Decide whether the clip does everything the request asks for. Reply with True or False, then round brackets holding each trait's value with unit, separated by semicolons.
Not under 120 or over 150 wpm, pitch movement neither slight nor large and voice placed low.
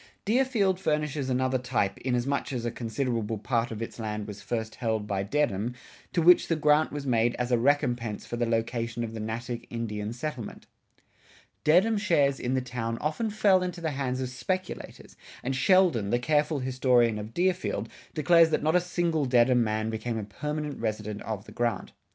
False (180 wpm; 5.0 semitones; 125 Hz)